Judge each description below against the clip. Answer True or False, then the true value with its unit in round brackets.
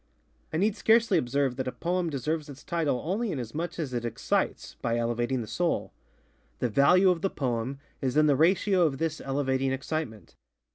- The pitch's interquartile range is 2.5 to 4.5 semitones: False (5.2 semitones)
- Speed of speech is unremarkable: True (180 wpm)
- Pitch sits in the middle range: True (145 Hz)